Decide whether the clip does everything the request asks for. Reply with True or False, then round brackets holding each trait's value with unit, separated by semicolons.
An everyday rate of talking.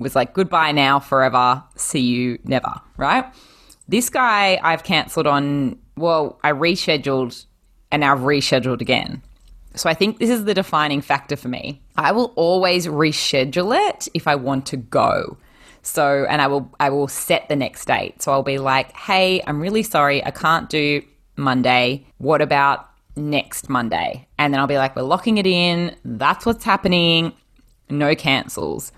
True (170 wpm)